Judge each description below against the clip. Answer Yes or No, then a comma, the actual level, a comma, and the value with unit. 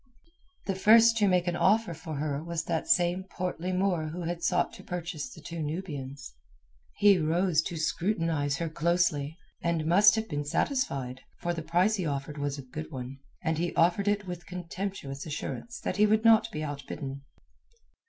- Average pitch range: Yes, average, 4.0 semitones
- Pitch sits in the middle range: Yes, medium, 170 Hz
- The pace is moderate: Yes, average, 180 wpm